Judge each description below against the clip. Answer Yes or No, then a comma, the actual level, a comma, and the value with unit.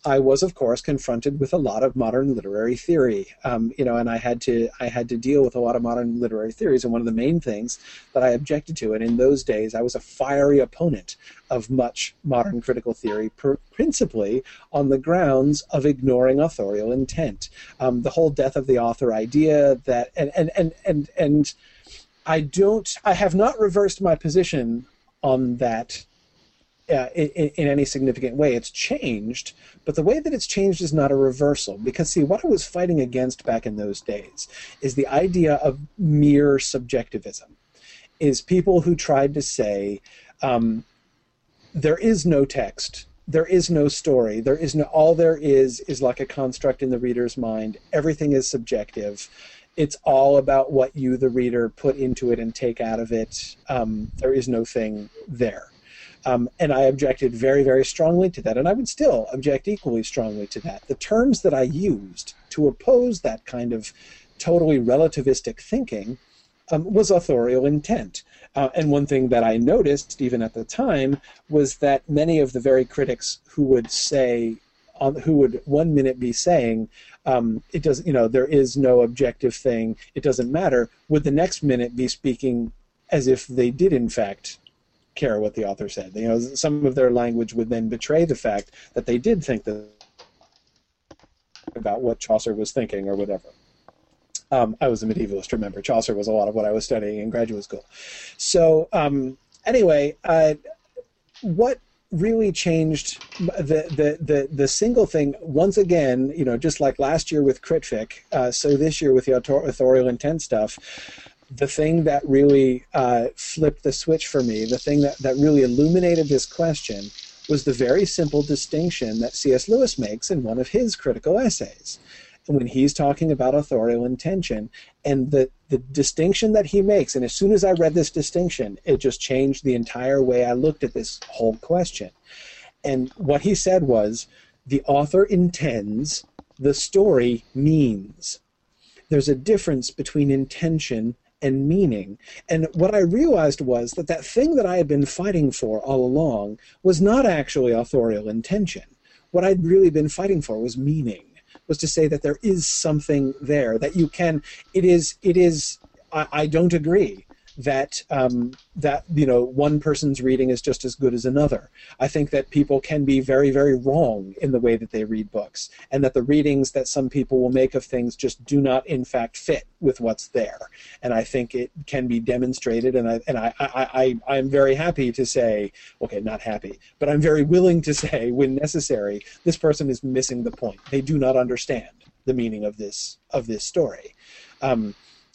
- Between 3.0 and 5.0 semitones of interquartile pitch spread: Yes, average, 4.3 semitones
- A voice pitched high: No, low, 135 Hz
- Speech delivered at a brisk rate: No, average, 185 wpm